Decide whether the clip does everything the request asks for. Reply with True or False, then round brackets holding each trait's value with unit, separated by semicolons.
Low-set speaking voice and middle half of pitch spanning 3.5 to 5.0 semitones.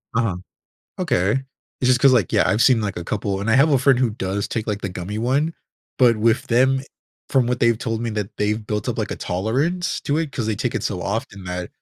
True (115 Hz; 4.0 semitones)